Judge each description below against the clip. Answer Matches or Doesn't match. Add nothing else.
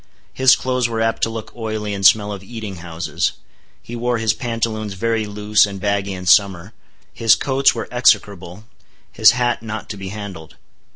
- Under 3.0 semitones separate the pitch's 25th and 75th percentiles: Matches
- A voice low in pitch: Matches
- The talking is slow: Doesn't match